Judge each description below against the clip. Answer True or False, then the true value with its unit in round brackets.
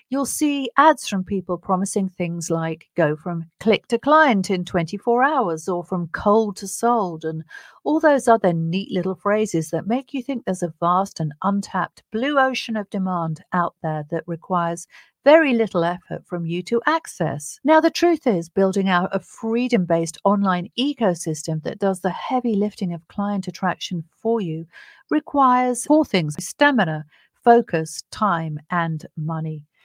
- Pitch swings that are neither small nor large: False (5.7 semitones)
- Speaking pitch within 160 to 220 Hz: True (190 Hz)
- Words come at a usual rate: True (165 wpm)